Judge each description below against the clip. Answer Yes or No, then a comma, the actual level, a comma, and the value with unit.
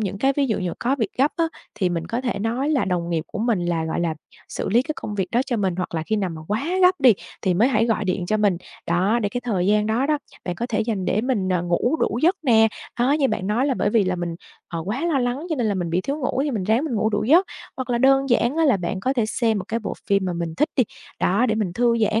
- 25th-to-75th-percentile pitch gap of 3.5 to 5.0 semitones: No, wide, 5.4 semitones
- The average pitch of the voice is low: No, high, 220 Hz